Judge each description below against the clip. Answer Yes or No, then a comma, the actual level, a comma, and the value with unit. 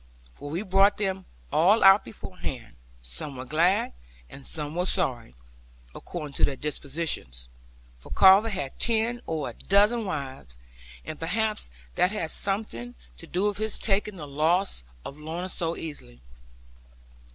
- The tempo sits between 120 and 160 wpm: Yes, average, 145 wpm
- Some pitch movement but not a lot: No, wide, 6.0 semitones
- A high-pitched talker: No, medium, 170 Hz